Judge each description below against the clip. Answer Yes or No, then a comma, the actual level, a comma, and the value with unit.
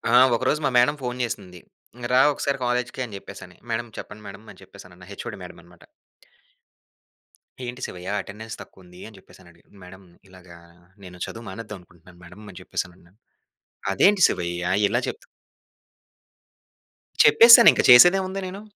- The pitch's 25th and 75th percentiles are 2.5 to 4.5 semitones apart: No, wide, 5.5 semitones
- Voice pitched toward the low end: Yes, low, 100 Hz